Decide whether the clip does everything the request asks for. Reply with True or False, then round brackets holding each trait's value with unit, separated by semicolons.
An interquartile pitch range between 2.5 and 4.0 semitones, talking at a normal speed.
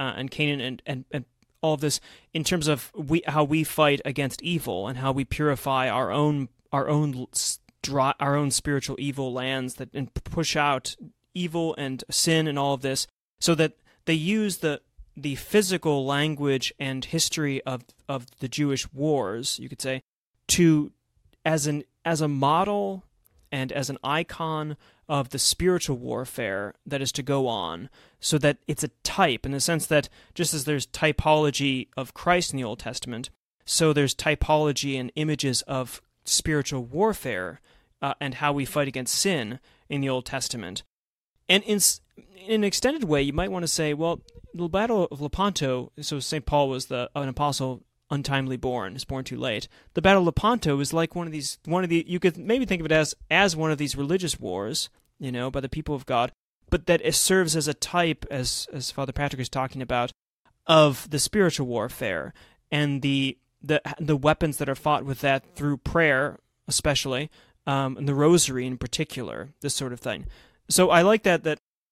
True (3.3 semitones; 185 wpm)